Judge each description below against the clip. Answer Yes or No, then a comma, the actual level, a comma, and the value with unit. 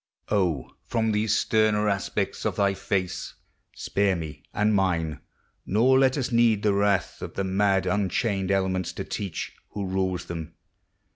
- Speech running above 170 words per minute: No, average, 150 wpm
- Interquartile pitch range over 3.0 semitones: No, narrow, 2.4 semitones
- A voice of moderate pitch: No, low, 100 Hz